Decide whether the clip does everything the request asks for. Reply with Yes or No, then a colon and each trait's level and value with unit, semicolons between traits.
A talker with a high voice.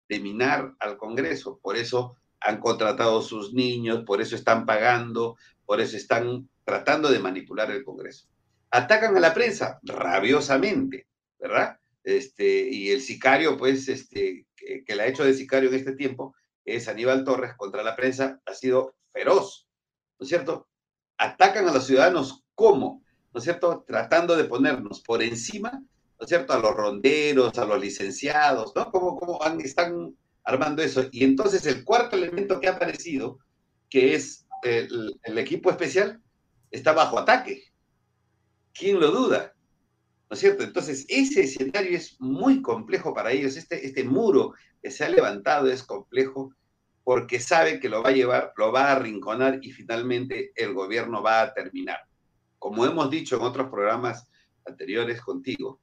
No: low, 135 Hz